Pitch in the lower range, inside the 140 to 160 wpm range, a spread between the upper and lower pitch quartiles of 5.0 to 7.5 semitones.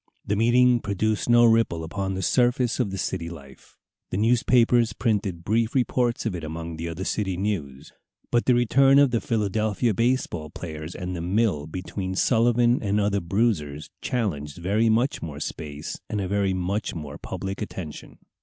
No: low, 100 Hz; average, 170 wpm; wide, 5.5 semitones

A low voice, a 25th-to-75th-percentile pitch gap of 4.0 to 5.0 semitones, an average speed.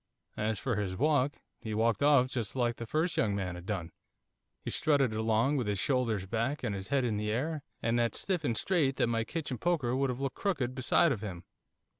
No: low, 120 Hz; average, 4.4 semitones; fast, 220 wpm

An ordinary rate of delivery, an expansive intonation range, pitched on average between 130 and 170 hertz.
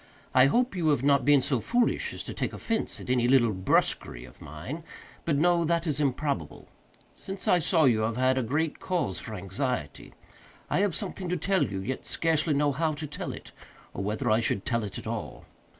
No: fast, 210 wpm; wide, 6.4 semitones; medium, 140 Hz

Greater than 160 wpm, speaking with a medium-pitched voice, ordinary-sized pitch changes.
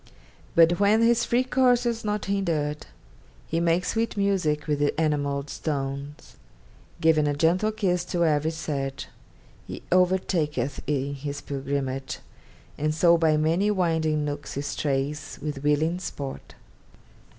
No: slow, 135 wpm; medium, 155 Hz; average, 4.1 semitones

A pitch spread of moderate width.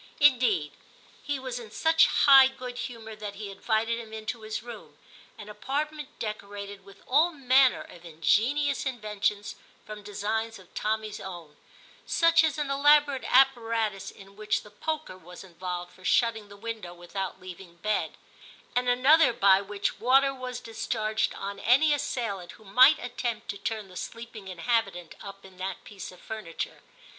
Yes: average, 4.5 semitones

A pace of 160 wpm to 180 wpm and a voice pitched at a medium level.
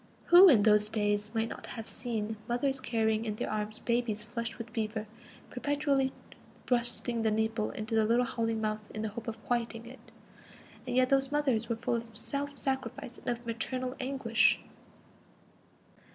No: average, 165 wpm; high, 230 Hz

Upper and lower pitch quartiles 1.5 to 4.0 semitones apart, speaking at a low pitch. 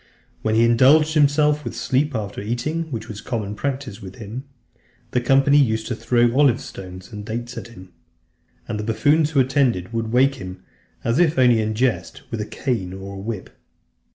No: average, 4.4 semitones; low, 120 Hz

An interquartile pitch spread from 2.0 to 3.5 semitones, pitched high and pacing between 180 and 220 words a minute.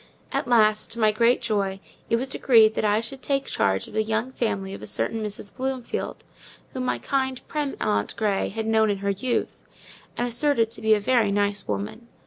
Yes: average, 3.1 semitones; high, 220 Hz; fast, 205 wpm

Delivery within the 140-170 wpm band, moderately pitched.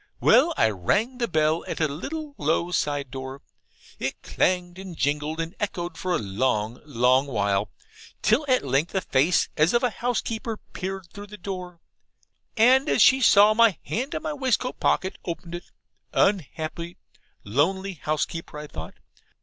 Yes: average, 160 wpm; medium, 175 Hz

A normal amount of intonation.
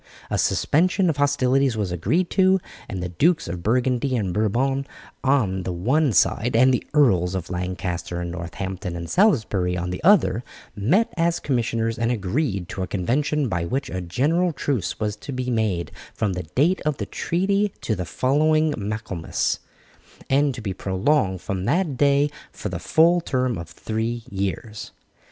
No: wide, 7.5 semitones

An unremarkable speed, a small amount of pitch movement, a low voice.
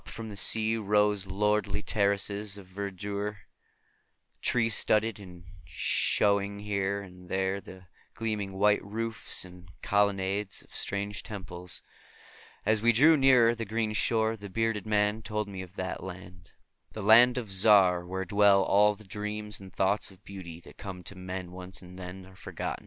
Yes: average, 160 wpm; narrow, 2.1 semitones; low, 100 Hz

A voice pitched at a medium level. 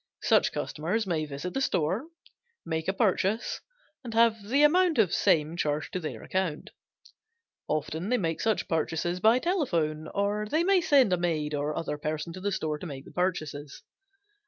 Yes: medium, 180 Hz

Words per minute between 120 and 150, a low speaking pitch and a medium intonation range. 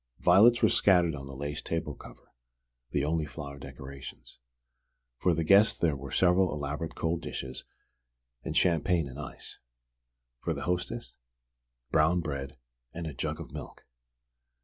Yes: average, 145 wpm; very low, 80 Hz; average, 3.8 semitones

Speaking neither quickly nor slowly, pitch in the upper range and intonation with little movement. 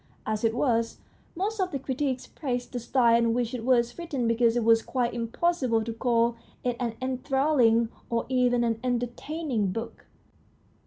Yes: average, 165 wpm; high, 240 Hz; narrow, 2.2 semitones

